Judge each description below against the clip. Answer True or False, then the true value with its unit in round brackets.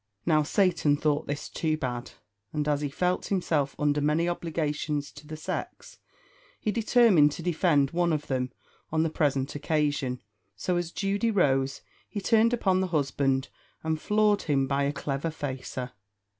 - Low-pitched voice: False (150 Hz)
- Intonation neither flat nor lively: True (3.7 semitones)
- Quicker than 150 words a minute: True (160 wpm)